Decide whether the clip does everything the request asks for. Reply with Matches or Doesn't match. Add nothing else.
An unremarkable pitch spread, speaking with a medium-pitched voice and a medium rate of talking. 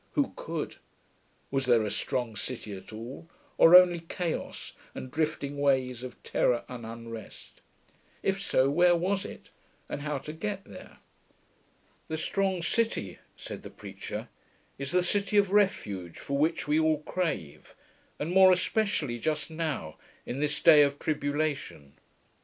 Doesn't match